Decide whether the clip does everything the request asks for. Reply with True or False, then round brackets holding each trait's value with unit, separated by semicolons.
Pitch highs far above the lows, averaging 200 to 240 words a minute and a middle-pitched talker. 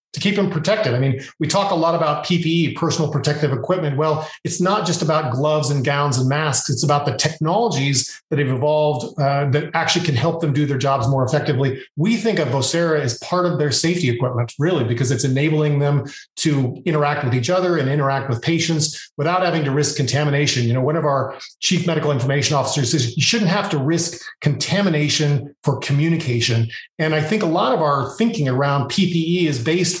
False (3.0 semitones; 205 wpm; 150 Hz)